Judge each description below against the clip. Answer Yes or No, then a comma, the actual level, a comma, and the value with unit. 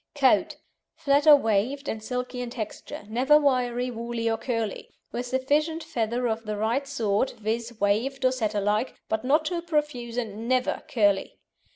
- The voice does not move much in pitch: No, average, 3.6 semitones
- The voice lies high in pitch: Yes, high, 245 Hz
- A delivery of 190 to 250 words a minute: No, average, 165 wpm